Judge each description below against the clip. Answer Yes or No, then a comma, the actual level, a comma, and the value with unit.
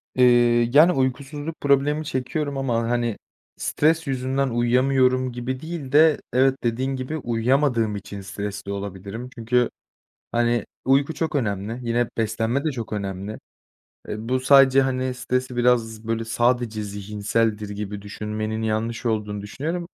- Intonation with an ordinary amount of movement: Yes, average, 3.5 semitones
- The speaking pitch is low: Yes, low, 120 Hz